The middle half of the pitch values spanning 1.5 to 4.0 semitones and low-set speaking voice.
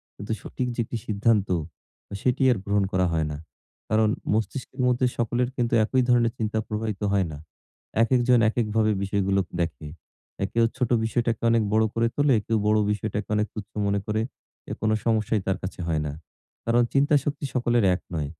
Yes: average, 2.9 semitones; low, 110 Hz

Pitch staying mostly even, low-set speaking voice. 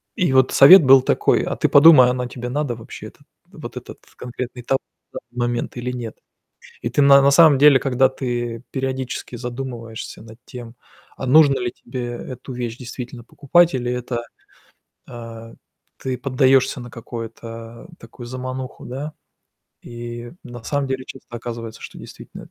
Yes: narrow, 1.9 semitones; low, 125 Hz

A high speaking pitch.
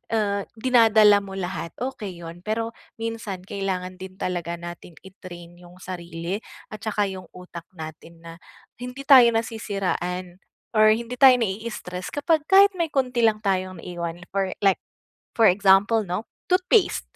Yes: high, 195 Hz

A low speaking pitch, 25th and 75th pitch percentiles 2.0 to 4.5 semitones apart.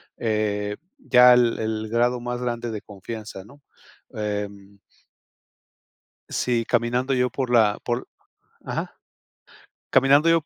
Yes: low, 120 Hz; average, 2.7 semitones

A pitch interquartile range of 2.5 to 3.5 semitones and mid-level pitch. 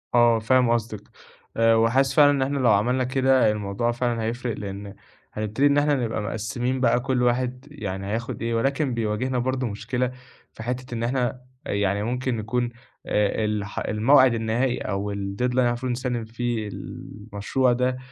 No: average, 3.0 semitones; low, 120 Hz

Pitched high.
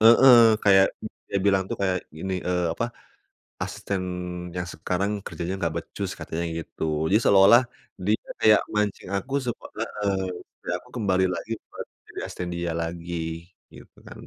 No: very low, 95 Hz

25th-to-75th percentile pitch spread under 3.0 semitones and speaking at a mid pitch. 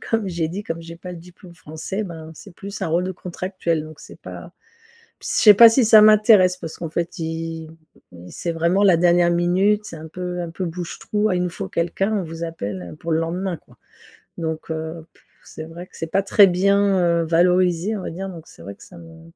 Yes: narrow, 2.6 semitones; medium, 175 Hz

